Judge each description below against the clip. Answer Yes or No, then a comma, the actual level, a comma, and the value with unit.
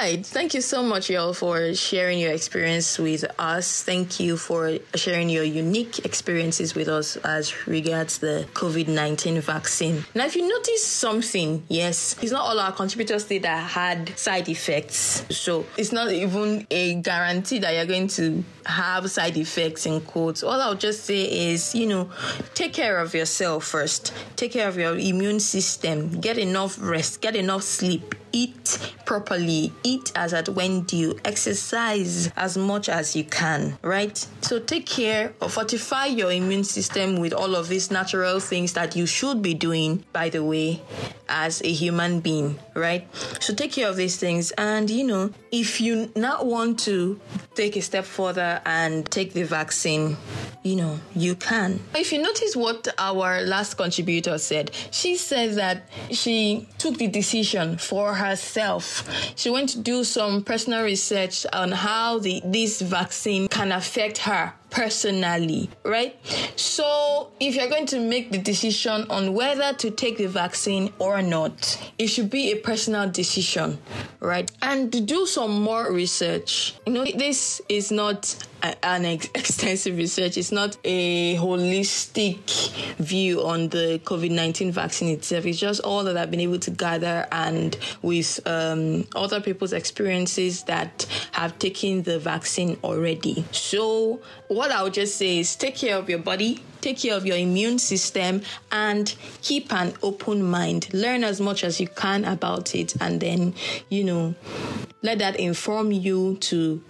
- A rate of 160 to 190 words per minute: Yes, average, 165 wpm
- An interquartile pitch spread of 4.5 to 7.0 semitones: No, average, 4.1 semitones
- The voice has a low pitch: No, high, 190 Hz